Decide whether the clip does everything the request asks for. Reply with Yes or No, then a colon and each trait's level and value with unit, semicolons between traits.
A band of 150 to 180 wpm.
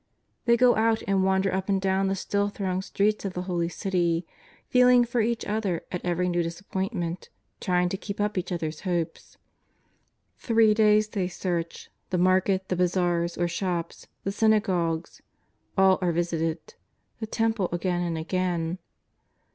Yes: average, 165 wpm